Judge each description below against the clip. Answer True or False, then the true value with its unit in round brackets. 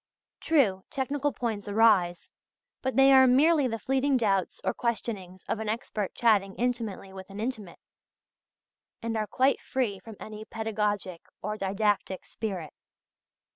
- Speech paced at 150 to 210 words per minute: False (135 wpm)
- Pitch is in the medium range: False (220 Hz)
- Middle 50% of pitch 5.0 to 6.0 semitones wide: False (4.3 semitones)